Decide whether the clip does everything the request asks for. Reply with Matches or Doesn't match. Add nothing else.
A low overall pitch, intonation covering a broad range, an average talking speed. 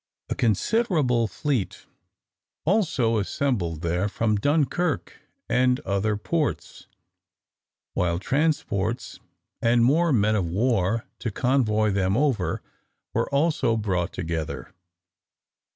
Doesn't match